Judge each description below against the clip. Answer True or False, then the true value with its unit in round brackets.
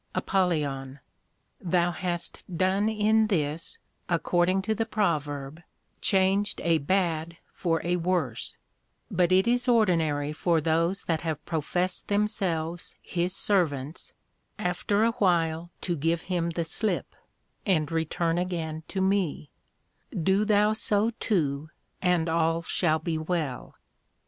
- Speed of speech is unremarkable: False (125 wpm)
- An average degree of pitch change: True (3.2 semitones)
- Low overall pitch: False (175 Hz)